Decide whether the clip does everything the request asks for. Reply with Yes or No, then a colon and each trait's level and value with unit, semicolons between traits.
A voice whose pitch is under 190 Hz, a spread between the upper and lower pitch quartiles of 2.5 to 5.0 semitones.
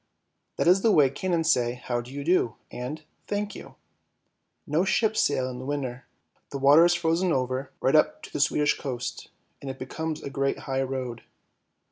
Yes: medium, 140 Hz; average, 4.2 semitones